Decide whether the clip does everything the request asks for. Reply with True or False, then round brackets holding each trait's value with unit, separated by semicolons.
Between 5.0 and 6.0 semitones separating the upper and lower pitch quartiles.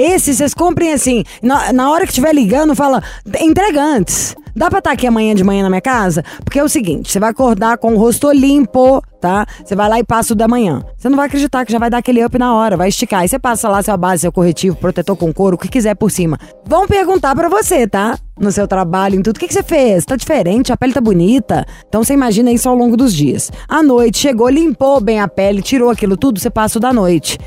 True (5.5 semitones)